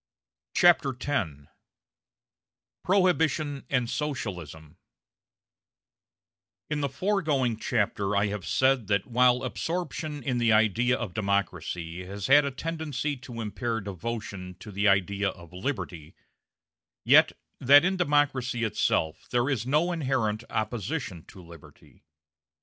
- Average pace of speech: No, slow, 115 wpm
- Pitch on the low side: Yes, low, 120 Hz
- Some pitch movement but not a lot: No, wide, 6.3 semitones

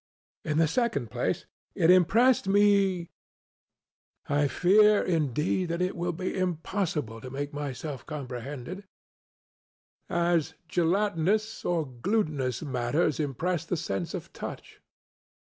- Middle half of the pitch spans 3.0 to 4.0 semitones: No, average, 4.5 semitones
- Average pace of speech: No, slow, 110 wpm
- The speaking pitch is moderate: Yes, medium, 165 Hz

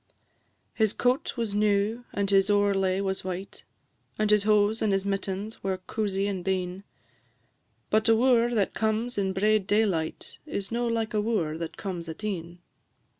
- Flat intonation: Yes, narrow, 2.2 semitones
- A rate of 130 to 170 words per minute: Yes, average, 165 wpm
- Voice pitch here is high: Yes, high, 205 Hz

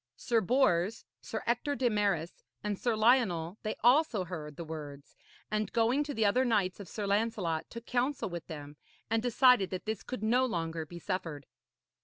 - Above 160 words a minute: Yes, average, 180 wpm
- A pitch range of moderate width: No, wide, 5.8 semitones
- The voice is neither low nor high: No, high, 210 Hz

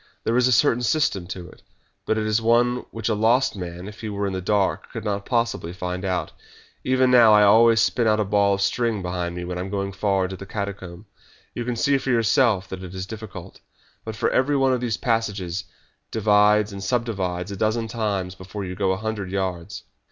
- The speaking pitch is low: Yes, low, 105 Hz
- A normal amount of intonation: Yes, average, 3.4 semitones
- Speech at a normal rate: No, fast, 220 wpm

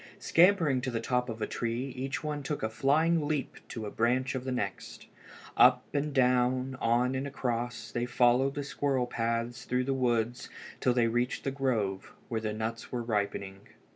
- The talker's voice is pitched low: Yes, low, 125 Hz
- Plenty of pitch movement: No, narrow, 2.6 semitones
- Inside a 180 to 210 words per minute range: Yes, average, 185 wpm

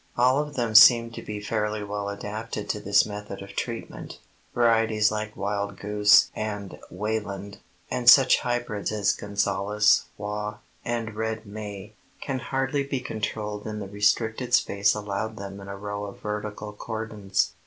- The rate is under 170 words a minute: Yes, average, 150 wpm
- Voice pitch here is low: Yes, low, 105 Hz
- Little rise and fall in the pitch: Yes, narrow, 1.7 semitones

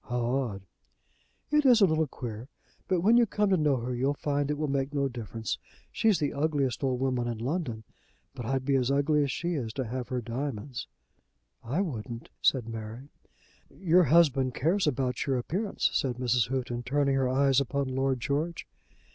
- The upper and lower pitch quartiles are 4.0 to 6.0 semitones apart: No, average, 3.4 semitones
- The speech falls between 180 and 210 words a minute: Yes, average, 185 wpm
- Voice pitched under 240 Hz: Yes, low, 135 Hz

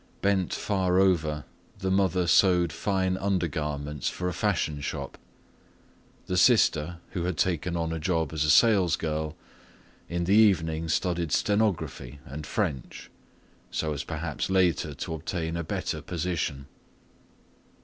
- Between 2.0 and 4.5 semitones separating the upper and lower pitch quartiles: Yes, average, 3.1 semitones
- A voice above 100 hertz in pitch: No, very low, 85 Hz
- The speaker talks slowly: Yes, slow, 130 wpm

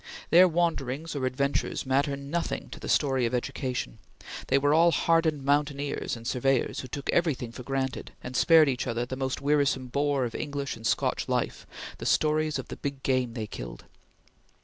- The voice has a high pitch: No, medium, 140 Hz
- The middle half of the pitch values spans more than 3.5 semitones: No, narrow, 2.6 semitones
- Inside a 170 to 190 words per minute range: Yes, average, 180 wpm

